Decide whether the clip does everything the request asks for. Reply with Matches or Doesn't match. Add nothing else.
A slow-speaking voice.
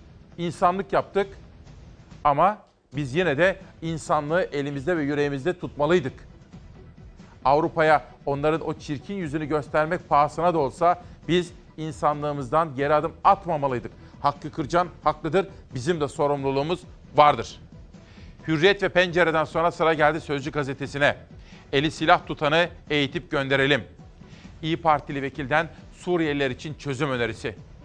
Doesn't match